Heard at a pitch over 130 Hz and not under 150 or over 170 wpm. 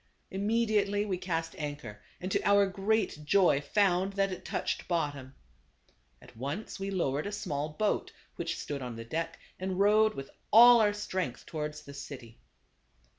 Yes: medium, 185 Hz; average, 165 wpm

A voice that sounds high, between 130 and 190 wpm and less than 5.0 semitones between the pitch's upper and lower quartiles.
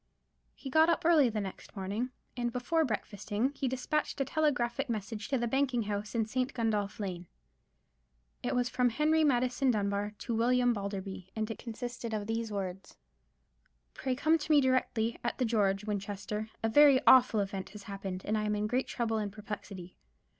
Yes: high, 225 Hz; average, 180 wpm; average, 3.7 semitones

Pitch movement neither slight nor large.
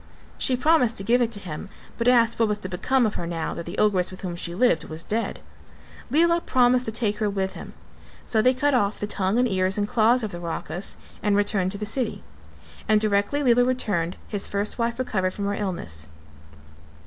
Yes: average, 4.4 semitones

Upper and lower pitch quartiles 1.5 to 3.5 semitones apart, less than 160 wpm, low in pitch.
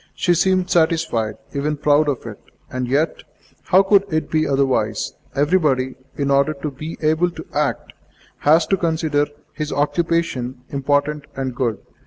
No: average, 3.2 semitones; average, 150 wpm; medium, 150 Hz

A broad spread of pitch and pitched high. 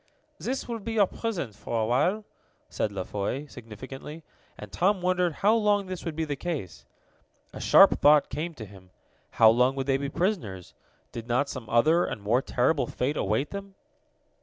No: wide, 7.8 semitones; medium, 140 Hz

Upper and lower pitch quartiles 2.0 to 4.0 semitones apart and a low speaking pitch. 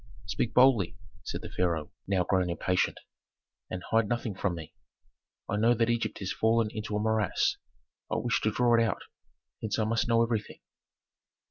Yes: average, 3.3 semitones; low, 110 Hz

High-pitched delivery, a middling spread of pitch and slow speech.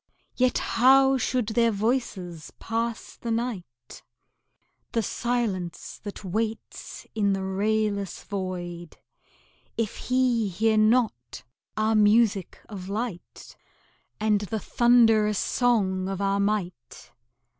Yes: high, 215 Hz; average, 3.3 semitones; slow, 105 wpm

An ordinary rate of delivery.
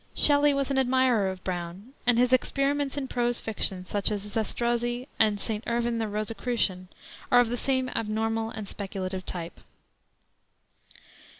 Yes: average, 145 wpm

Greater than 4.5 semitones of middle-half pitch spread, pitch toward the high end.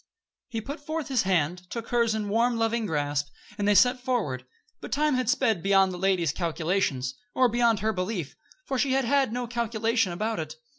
Yes: average, 5.3 semitones; high, 220 Hz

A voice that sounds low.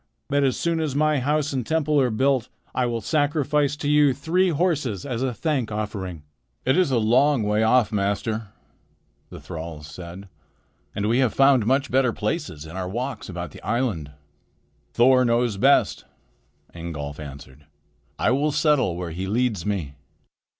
Yes: low, 120 Hz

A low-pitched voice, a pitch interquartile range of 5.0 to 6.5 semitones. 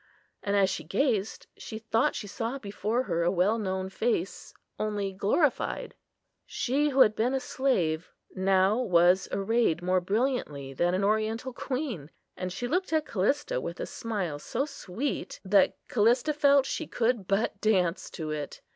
No: high, 215 Hz; average, 5.3 semitones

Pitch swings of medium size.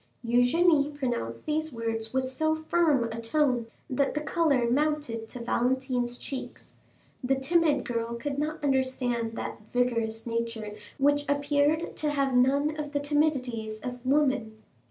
Yes: average, 3.9 semitones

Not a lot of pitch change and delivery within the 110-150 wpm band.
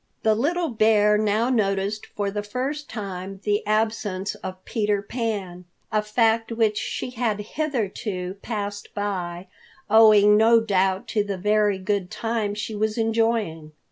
Yes: narrow, 2.1 semitones; average, 140 wpm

